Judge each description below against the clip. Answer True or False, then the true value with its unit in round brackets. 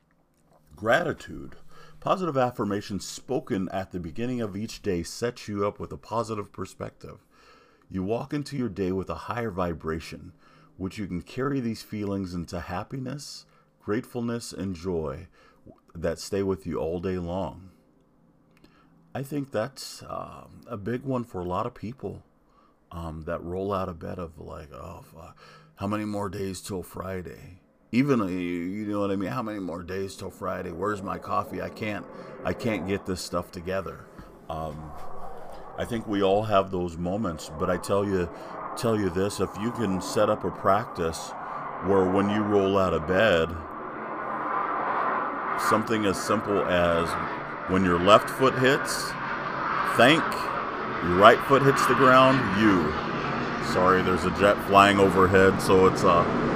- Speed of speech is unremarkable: True (160 wpm)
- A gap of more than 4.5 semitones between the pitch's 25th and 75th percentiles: False (3.2 semitones)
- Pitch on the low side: True (95 Hz)